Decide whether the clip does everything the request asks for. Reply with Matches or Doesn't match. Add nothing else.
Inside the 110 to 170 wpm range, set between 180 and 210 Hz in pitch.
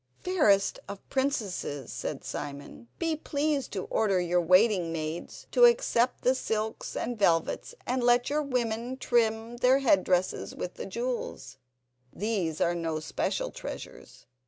Doesn't match